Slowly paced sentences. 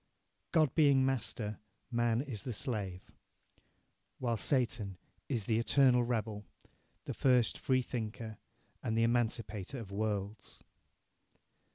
Yes: slow, 105 wpm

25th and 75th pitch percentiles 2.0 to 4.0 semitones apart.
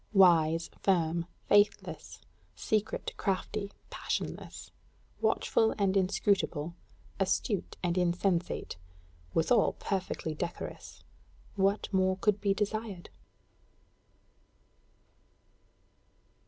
Yes: average, 2.8 semitones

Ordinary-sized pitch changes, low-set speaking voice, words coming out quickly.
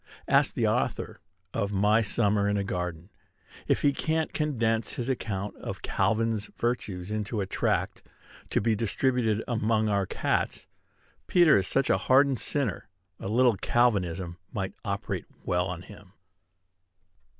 No: average, 3.4 semitones; low, 105 Hz; average, 140 wpm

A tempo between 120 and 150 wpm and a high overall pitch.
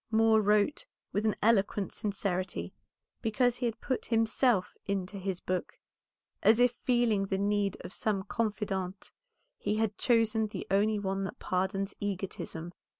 Yes: average, 145 wpm; high, 205 Hz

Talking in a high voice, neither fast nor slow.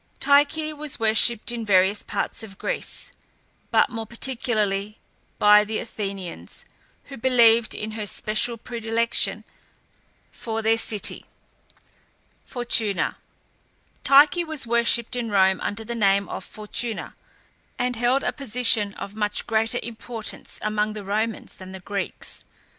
No: high, 225 Hz; slow, 125 wpm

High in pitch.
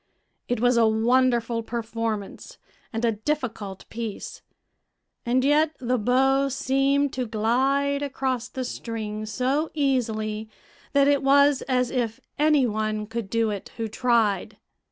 Yes: high, 245 Hz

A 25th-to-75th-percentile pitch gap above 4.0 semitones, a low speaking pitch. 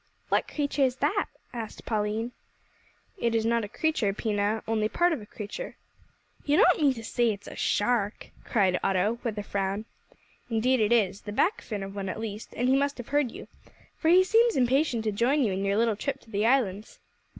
No: average, 4.5 semitones; high, 225 Hz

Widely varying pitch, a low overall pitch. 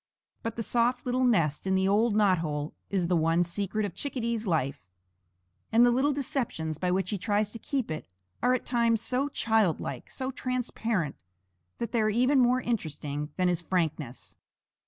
No: wide, 6.1 semitones; high, 210 Hz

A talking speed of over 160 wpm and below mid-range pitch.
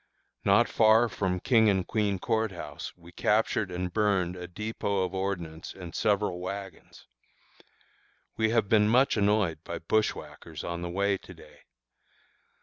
No: average, 145 wpm; low, 100 Hz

